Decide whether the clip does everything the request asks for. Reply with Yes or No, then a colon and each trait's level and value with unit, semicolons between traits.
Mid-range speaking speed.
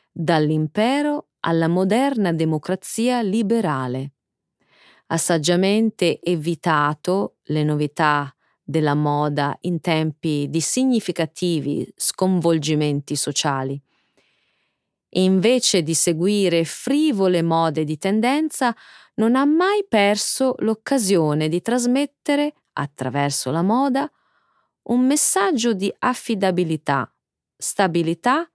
No: slow, 90 wpm